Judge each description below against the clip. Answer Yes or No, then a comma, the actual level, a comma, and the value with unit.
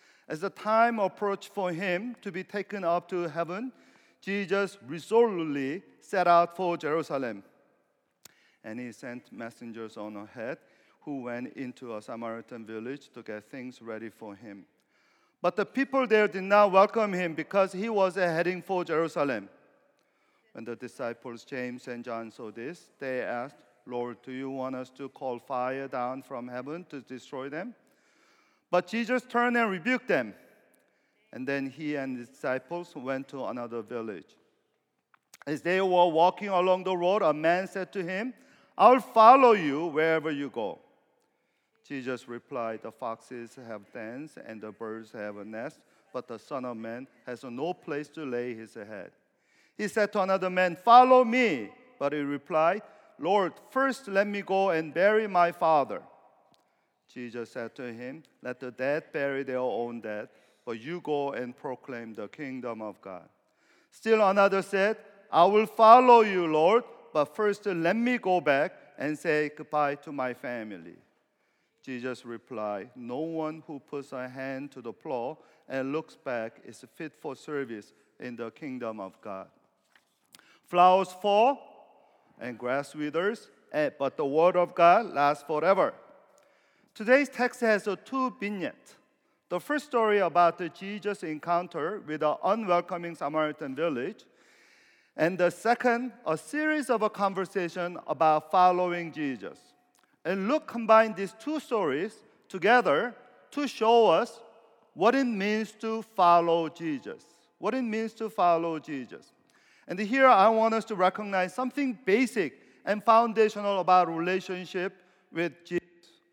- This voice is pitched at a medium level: Yes, medium, 175 Hz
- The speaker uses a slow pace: No, average, 150 wpm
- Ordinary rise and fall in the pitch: No, wide, 7.5 semitones